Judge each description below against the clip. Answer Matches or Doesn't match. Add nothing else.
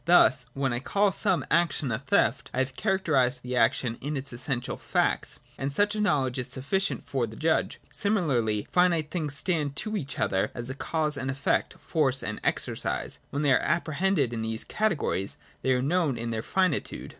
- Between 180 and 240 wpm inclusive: Matches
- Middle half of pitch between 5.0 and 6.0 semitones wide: Matches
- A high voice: Doesn't match